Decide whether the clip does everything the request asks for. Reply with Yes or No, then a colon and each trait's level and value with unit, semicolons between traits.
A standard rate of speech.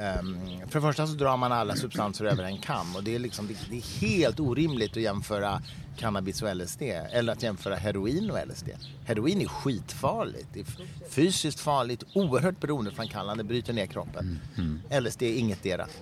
Yes: average, 170 wpm